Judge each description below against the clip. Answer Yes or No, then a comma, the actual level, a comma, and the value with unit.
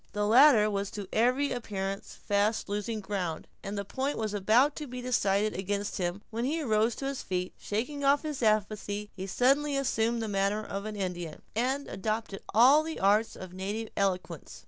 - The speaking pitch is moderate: No, high, 215 Hz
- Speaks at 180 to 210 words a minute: Yes, average, 190 wpm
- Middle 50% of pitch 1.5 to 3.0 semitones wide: No, average, 4.0 semitones